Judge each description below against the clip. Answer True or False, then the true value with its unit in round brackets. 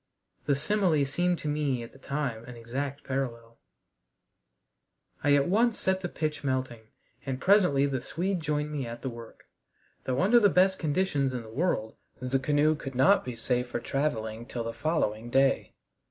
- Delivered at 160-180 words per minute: True (175 wpm)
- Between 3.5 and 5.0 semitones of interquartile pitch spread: True (4.1 semitones)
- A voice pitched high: False (140 Hz)